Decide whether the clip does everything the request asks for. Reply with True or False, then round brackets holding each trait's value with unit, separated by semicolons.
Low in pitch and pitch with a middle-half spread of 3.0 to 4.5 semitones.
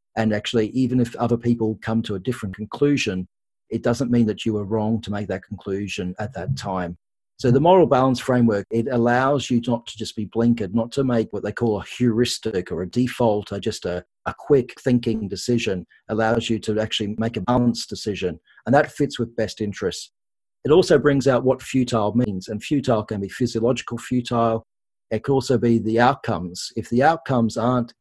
False (115 Hz; 2.5 semitones)